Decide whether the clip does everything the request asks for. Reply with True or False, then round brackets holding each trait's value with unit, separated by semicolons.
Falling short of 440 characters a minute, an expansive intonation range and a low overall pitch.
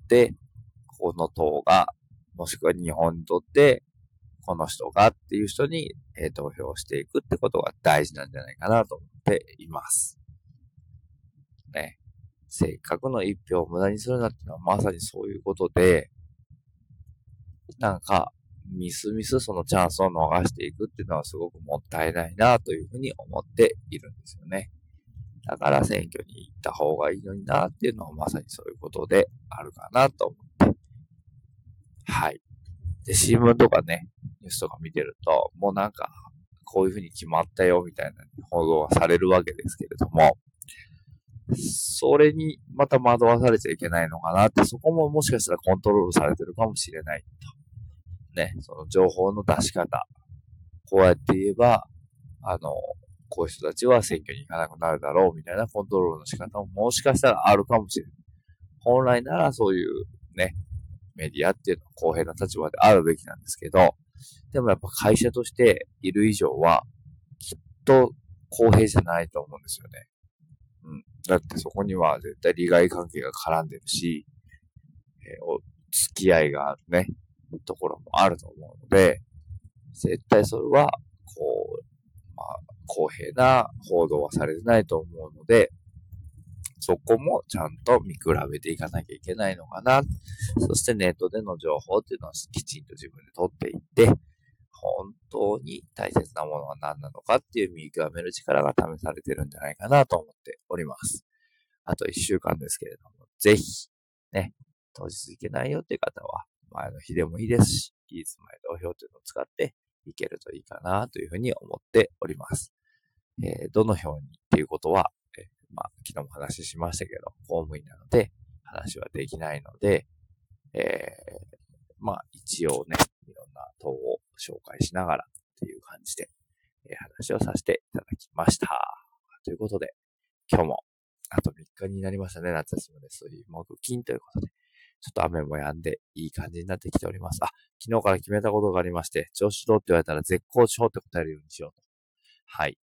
True (345 characters per minute; 7.4 semitones; 105 Hz)